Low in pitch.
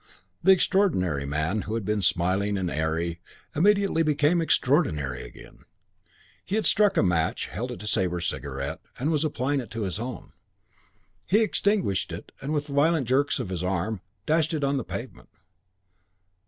Yes: low, 110 Hz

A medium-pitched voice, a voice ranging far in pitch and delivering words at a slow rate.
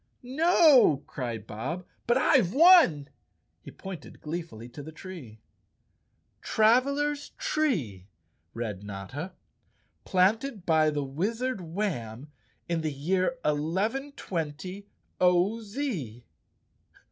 Yes: medium, 175 Hz; wide, 8.6 semitones; slow, 110 wpm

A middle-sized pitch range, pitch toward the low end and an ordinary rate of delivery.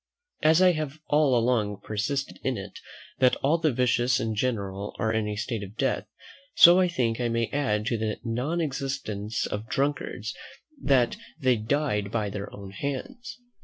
Yes: average, 4.8 semitones; low, 120 Hz; average, 170 wpm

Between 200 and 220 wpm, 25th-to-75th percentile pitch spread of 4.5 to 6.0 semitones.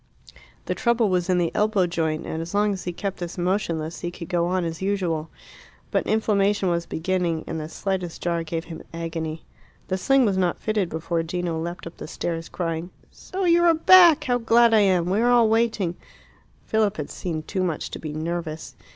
No: fast, 205 wpm; average, 4.0 semitones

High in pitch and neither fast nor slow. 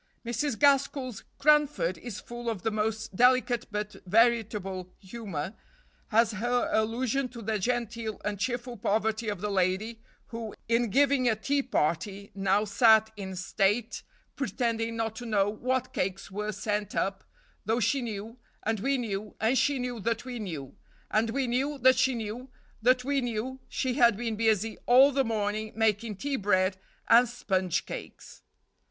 Yes: high, 225 Hz; average, 160 wpm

